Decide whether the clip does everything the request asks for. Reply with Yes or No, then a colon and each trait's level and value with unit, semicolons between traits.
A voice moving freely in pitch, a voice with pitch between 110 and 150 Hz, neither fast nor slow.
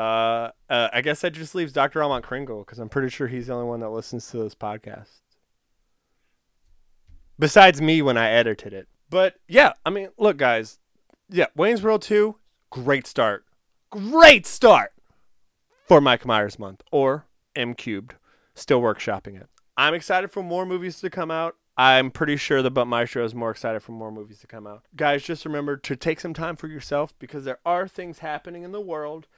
Yes: wide, 6.4 semitones; medium, 140 Hz; average, 190 wpm